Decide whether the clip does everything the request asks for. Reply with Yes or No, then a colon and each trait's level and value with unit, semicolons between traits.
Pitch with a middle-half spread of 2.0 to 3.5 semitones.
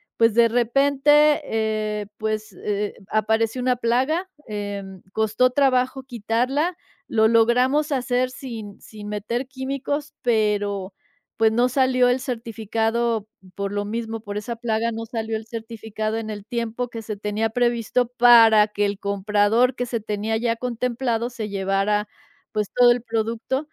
Yes: average, 2.7 semitones